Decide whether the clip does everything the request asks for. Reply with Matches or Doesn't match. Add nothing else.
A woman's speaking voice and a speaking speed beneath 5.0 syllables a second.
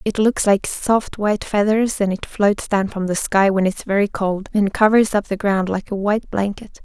Matches